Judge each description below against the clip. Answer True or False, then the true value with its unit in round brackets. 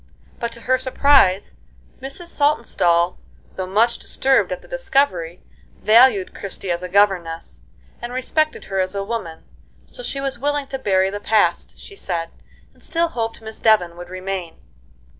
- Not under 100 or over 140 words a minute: False (160 wpm)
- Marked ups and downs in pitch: True (6.3 semitones)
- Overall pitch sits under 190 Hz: False (215 Hz)